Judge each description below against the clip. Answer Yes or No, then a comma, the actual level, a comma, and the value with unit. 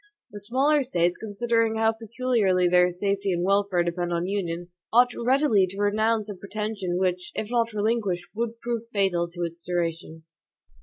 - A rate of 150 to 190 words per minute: Yes, average, 160 wpm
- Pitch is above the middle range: Yes, high, 200 Hz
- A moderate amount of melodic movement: Yes, average, 4.2 semitones